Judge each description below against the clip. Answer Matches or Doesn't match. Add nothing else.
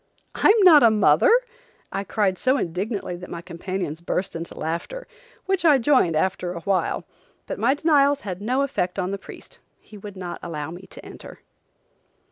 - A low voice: Doesn't match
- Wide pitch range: Matches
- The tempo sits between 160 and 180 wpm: Matches